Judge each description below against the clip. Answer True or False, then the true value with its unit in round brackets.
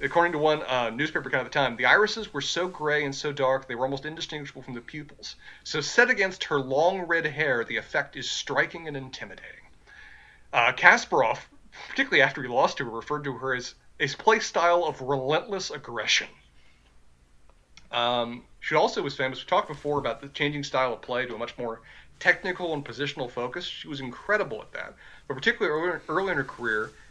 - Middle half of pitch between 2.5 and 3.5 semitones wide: False (4.4 semitones)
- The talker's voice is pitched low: False (145 Hz)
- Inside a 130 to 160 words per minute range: False (195 wpm)